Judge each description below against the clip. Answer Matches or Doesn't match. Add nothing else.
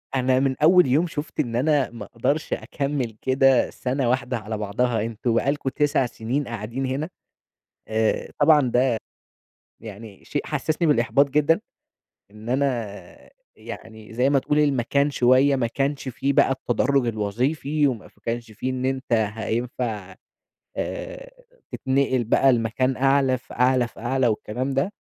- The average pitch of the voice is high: Doesn't match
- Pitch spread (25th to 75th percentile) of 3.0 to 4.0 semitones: Matches